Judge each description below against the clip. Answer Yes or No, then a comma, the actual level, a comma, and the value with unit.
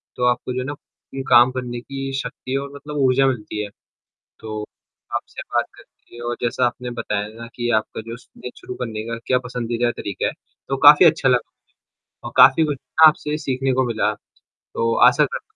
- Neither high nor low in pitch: No, low, 125 Hz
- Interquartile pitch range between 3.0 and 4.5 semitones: No, narrow, 2.5 semitones